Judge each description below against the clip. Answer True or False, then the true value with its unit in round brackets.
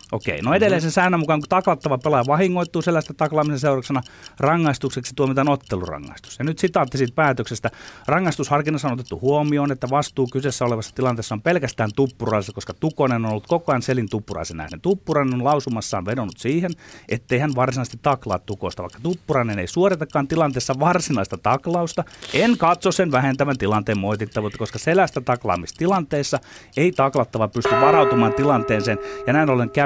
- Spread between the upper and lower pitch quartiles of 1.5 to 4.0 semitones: False (5.3 semitones)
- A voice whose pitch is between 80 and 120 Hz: False (135 Hz)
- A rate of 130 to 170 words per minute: True (155 wpm)